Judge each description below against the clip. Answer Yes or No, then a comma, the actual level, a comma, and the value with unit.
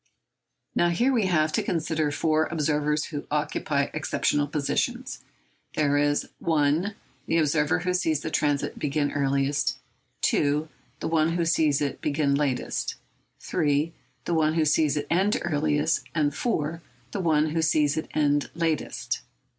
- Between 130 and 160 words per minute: Yes, average, 150 wpm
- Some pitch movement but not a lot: No, narrow, 1.9 semitones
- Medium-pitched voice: Yes, medium, 155 Hz